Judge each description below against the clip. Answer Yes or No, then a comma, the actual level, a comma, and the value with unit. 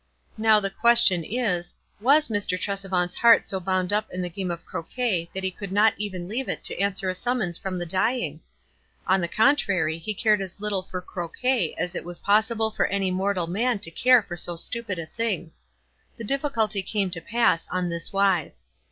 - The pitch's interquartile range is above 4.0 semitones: No, average, 3.7 semitones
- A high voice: Yes, high, 195 Hz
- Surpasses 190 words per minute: Yes, average, 200 wpm